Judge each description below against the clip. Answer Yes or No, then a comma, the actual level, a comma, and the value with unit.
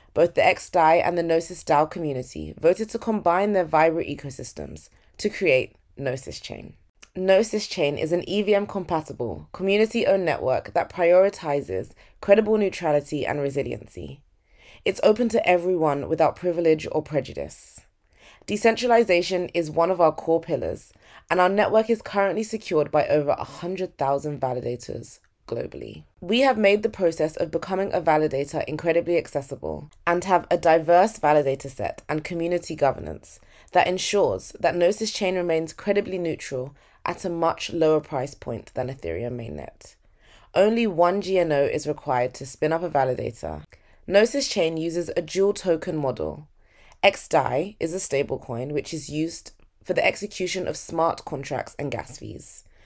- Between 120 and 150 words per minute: Yes, average, 145 wpm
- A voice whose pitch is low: No, medium, 165 Hz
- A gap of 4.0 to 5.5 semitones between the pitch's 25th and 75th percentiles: Yes, average, 4.9 semitones